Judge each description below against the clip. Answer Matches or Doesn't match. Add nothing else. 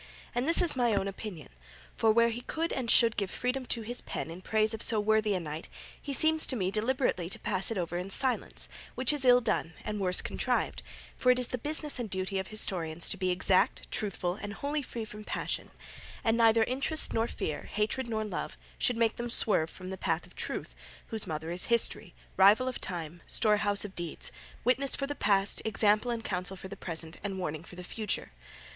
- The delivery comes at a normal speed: Doesn't match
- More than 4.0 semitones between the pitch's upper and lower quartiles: Matches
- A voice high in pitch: Matches